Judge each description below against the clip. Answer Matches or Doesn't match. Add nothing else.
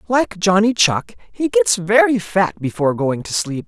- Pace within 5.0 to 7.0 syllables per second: Doesn't match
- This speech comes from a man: Matches